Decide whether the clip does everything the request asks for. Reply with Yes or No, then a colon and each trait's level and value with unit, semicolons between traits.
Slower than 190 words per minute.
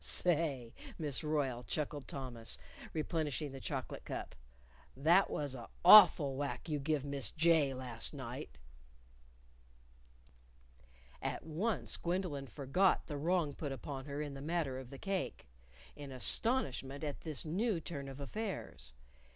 Yes: slow, 135 wpm